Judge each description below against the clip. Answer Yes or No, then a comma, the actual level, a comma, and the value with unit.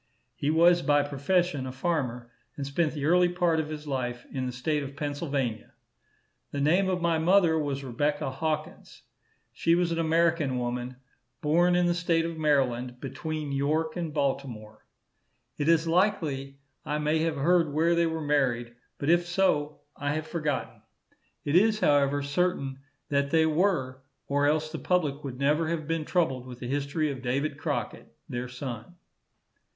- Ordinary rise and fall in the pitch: Yes, average, 3.3 semitones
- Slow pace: No, average, 165 wpm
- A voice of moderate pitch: Yes, medium, 150 Hz